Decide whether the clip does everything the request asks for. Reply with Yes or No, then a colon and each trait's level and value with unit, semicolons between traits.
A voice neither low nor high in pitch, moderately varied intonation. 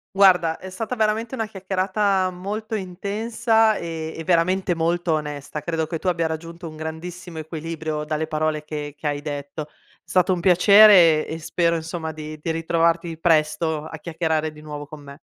Yes: medium, 165 Hz; average, 3.0 semitones